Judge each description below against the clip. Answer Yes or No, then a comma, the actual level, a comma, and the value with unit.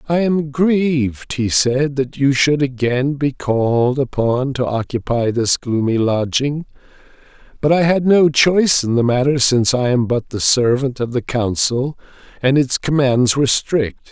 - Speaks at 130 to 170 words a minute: Yes, average, 165 wpm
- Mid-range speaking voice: No, low, 130 Hz